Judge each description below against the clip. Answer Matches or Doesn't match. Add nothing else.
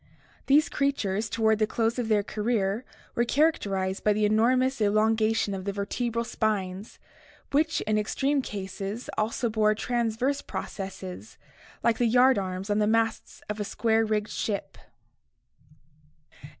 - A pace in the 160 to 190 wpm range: Doesn't match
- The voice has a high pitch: Matches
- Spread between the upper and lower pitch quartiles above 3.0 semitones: Doesn't match